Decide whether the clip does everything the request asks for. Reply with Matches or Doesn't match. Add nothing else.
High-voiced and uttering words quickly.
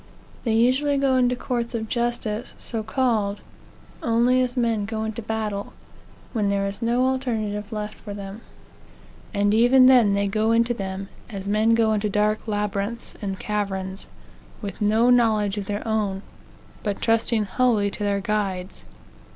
Doesn't match